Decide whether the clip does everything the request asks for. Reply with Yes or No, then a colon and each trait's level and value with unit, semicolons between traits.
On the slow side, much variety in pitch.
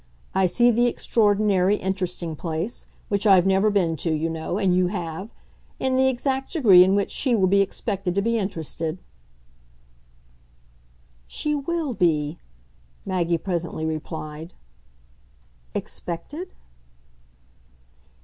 No: slow, 120 wpm; average, 4.7 semitones